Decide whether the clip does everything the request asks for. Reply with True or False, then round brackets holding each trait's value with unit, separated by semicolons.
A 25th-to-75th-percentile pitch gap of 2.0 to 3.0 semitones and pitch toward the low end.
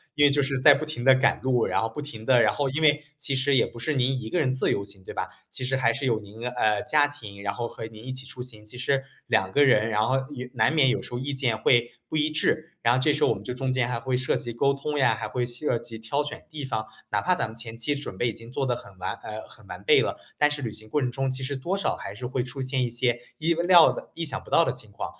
False (3.6 semitones; 130 Hz)